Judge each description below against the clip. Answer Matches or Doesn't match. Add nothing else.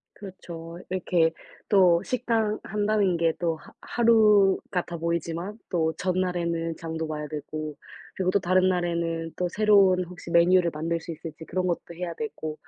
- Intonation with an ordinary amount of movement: Doesn't match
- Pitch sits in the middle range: Matches